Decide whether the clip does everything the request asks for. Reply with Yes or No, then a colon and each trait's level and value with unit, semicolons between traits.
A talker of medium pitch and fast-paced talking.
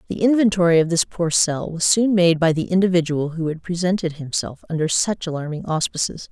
No: medium, 170 Hz; average, 190 wpm